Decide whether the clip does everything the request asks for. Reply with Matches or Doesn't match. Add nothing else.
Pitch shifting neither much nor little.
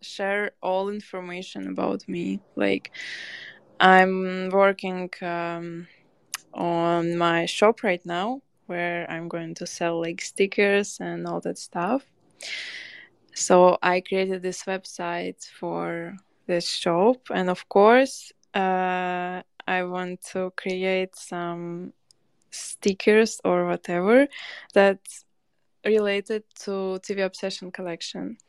Doesn't match